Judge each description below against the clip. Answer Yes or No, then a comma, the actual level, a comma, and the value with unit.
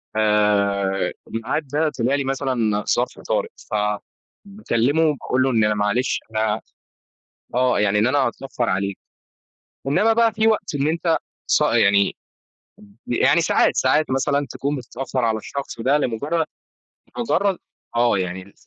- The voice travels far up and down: Yes, wide, 5.7 semitones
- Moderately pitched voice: No, low, 125 Hz